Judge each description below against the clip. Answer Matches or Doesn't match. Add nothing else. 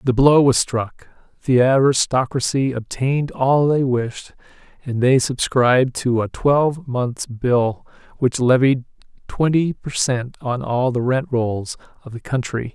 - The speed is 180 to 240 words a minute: Doesn't match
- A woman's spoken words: Doesn't match